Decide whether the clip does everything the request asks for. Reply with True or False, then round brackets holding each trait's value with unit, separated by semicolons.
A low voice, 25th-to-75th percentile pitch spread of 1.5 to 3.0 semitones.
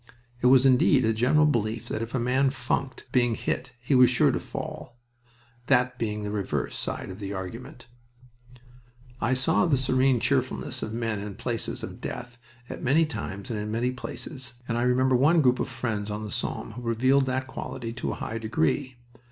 True (125 Hz; 2.6 semitones)